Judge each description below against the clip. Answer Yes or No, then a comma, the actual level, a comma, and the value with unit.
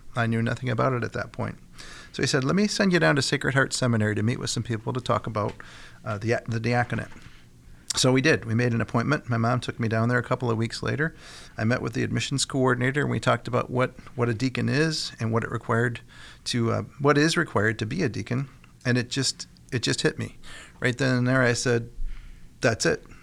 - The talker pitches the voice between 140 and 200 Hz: No, low, 120 Hz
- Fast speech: Yes, fast, 240 wpm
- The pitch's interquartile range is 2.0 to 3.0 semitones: Yes, narrow, 2.5 semitones